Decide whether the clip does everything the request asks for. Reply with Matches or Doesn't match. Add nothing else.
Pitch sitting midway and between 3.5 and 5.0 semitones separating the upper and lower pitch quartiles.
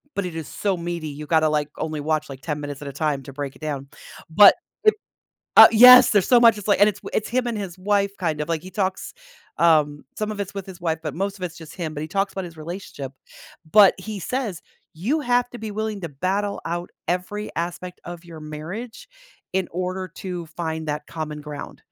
Matches